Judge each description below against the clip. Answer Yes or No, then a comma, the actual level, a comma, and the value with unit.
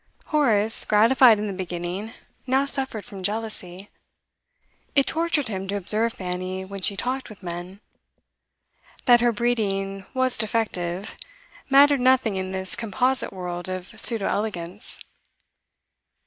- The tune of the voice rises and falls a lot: No, average, 4.5 semitones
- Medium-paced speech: No, slow, 125 wpm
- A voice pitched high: Yes, high, 210 Hz